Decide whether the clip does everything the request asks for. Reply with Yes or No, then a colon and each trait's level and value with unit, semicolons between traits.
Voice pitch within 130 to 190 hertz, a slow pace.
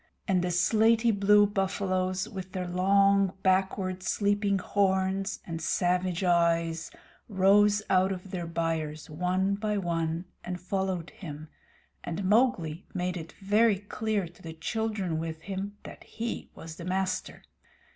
Yes: medium, 185 Hz; slow, 130 wpm